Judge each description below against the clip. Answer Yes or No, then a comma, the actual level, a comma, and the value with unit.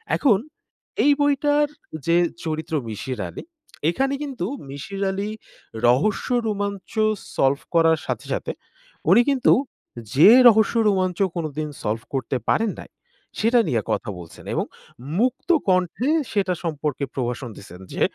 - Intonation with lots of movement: Yes, wide, 8.1 semitones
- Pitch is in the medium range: Yes, medium, 180 Hz